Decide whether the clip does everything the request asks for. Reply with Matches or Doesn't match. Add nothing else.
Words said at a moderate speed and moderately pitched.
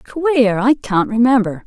Doesn't match